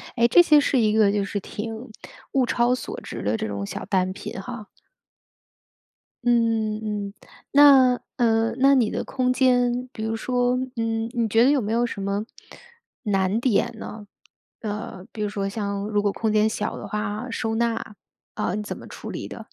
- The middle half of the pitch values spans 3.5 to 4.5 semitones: No, average, 2.8 semitones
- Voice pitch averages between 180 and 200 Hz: No, high, 225 Hz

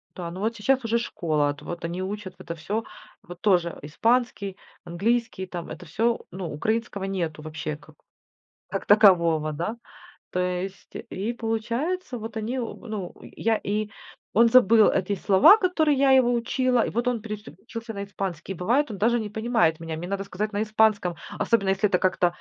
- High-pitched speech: Yes, high, 205 Hz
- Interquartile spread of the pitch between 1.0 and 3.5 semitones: No, average, 4.4 semitones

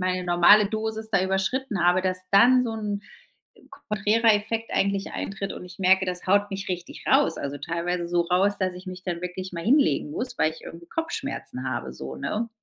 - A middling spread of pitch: Yes, average, 3.2 semitones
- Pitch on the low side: No, high, 190 Hz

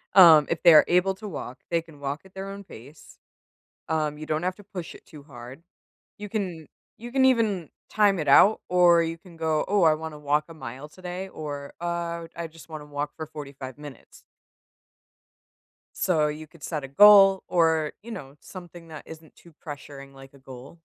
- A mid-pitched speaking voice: Yes, medium, 160 Hz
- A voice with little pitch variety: No, average, 3.5 semitones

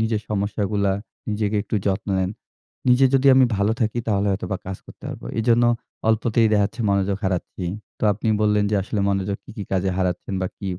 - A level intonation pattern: Yes, narrow, 2.2 semitones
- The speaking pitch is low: Yes, low, 105 Hz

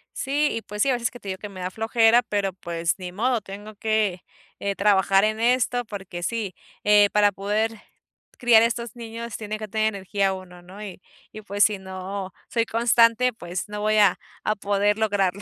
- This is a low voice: No, high, 210 Hz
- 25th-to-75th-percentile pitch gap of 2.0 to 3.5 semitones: Yes, narrow, 2.6 semitones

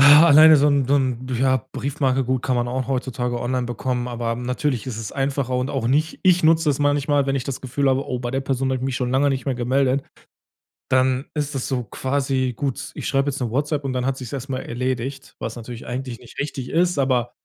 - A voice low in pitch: Yes, low, 130 Hz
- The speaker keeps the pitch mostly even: Yes, narrow, 2.0 semitones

